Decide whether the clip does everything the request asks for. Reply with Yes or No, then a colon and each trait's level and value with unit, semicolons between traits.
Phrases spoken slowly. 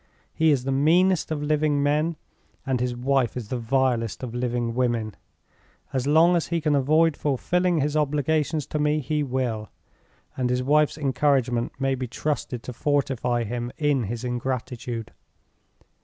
No: average, 155 wpm